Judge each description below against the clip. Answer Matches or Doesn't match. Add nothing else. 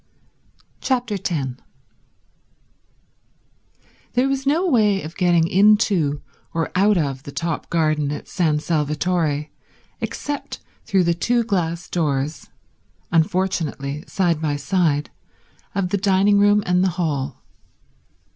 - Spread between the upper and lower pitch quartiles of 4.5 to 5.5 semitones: Matches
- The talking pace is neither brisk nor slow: Doesn't match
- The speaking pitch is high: Doesn't match